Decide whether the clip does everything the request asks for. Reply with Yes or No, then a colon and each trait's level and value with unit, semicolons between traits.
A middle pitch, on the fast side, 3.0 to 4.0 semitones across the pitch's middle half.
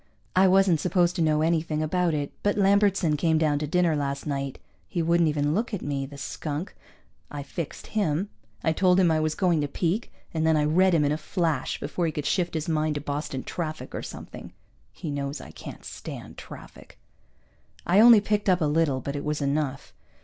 Yes: medium, 160 Hz; fast, 210 wpm; average, 3.4 semitones